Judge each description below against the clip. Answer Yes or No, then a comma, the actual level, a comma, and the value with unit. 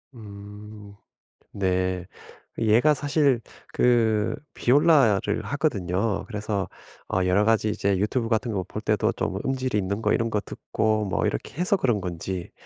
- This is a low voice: Yes, low, 105 Hz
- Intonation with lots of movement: No, average, 3.6 semitones